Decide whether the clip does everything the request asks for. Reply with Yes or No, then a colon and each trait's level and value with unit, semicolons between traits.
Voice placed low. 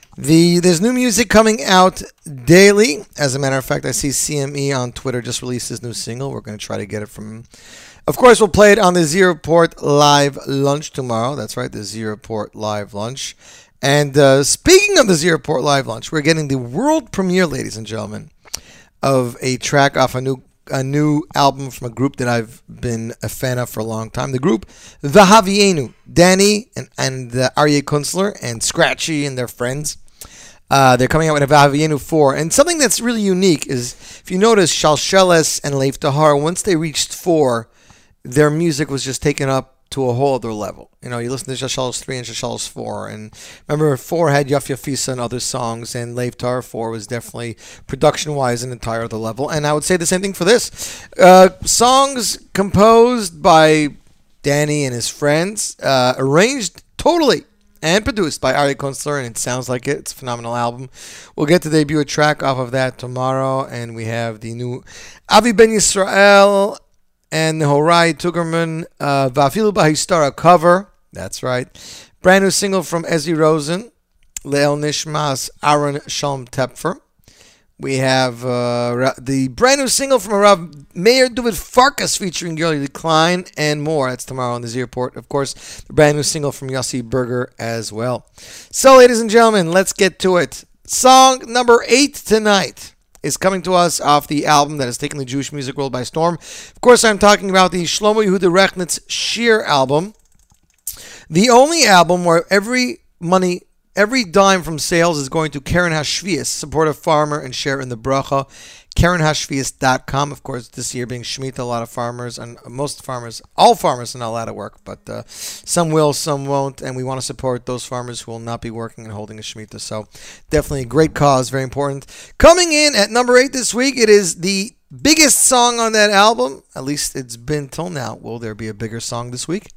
No: medium, 145 Hz